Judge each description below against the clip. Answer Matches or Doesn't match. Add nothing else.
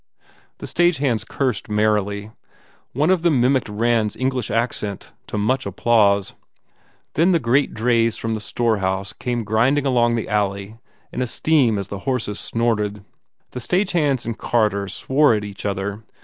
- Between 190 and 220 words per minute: Doesn't match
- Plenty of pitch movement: Doesn't match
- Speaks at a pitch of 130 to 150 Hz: Doesn't match